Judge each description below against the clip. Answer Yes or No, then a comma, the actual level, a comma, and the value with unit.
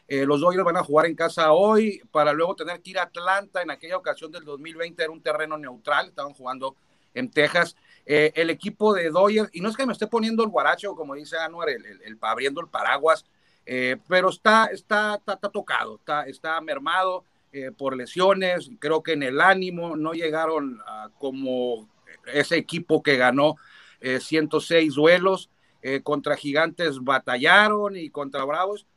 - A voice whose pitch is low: No, medium, 160 Hz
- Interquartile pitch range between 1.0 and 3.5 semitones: No, average, 4.2 semitones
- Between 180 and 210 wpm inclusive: Yes, average, 185 wpm